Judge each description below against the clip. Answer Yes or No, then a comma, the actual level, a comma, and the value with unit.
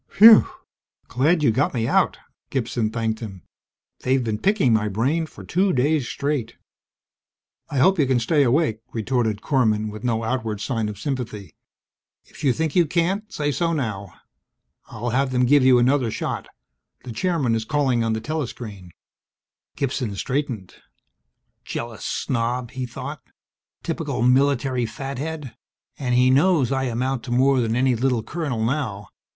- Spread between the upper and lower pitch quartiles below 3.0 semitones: No, average, 4.0 semitones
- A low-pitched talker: Yes, low, 125 Hz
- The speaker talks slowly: No, average, 155 wpm